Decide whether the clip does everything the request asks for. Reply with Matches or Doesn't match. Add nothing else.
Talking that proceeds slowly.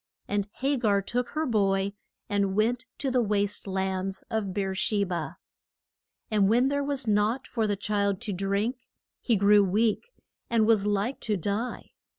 Doesn't match